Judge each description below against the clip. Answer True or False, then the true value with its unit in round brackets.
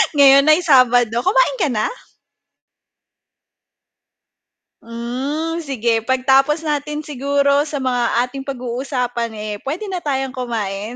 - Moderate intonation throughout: True (3.5 semitones)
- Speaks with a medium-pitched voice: False (270 Hz)